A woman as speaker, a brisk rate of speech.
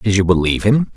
No: male; fast, 250 wpm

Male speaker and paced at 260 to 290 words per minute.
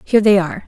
No: female; fast, 265 wpm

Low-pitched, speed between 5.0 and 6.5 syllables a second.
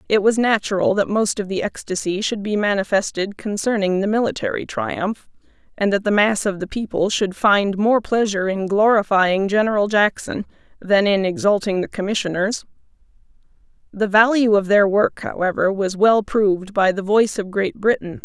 No: high, 205 Hz; 5.1 syllables/s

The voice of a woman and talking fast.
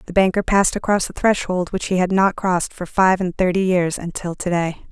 Yes: female; fast, 230 wpm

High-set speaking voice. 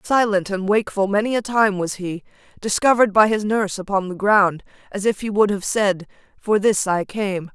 Yes: high, 205 Hz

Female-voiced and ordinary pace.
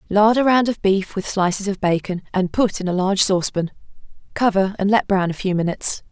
No: female; fast, 215 wpm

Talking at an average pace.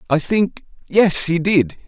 No: slow, 130 wpm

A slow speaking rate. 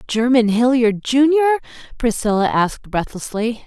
Yes: slow, 100 wpm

